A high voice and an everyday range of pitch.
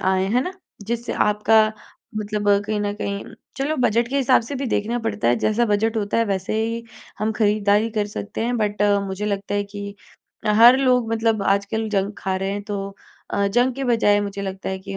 No: high, 210 Hz; narrow, 2.3 semitones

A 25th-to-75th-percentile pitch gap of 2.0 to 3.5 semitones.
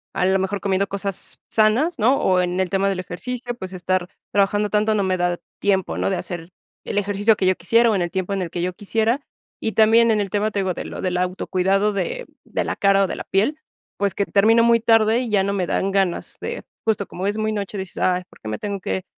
Yes: narrow, 2.6 semitones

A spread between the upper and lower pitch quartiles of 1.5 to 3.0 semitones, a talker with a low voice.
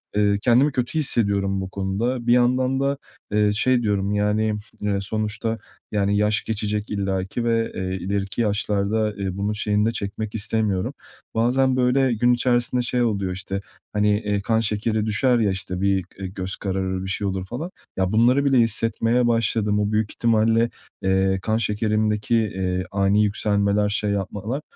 Yes: average, 2.7 semitones; low, 105 Hz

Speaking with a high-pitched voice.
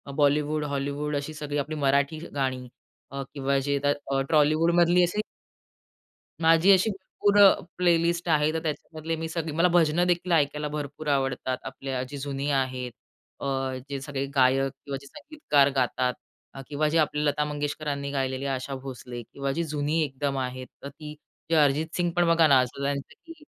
No: medium, 145 Hz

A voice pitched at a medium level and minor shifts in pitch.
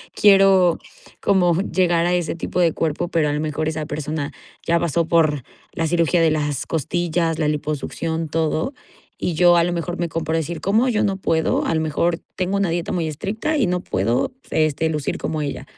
Yes: medium, 165 Hz; narrow, 2.2 semitones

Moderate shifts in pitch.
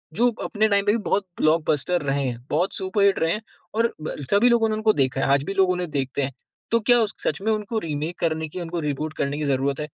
No: wide, 6.4 semitones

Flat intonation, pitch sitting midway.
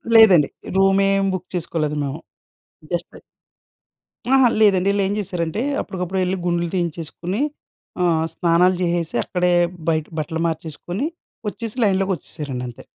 No: average, 3.0 semitones; medium, 180 Hz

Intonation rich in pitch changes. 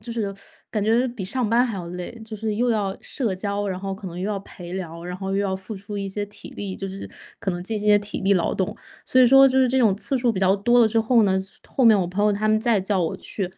No: average, 3.1 semitones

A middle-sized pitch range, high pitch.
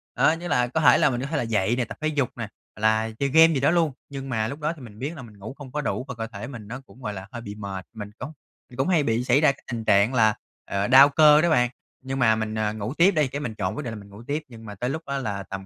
No: average, 4.7 semitones; low, 125 Hz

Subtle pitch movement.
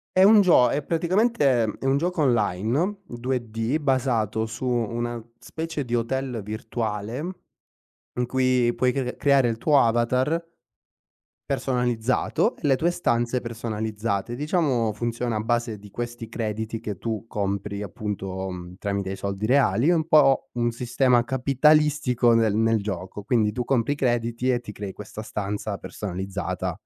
No: average, 3.7 semitones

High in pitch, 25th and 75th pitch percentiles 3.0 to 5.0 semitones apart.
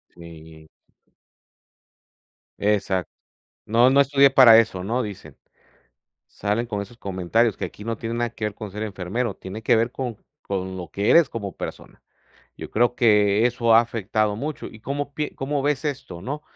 No: low, 110 Hz; average, 3.6 semitones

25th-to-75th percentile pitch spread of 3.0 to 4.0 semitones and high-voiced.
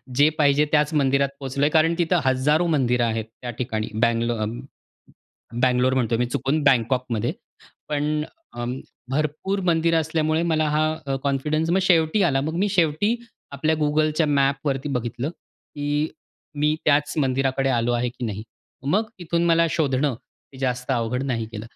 No: average, 3.5 semitones; medium, 145 Hz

